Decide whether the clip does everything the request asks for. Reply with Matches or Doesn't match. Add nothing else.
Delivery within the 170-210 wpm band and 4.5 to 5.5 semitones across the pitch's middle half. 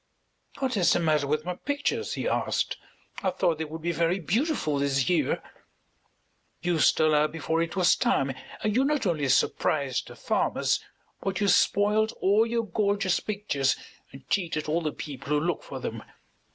Matches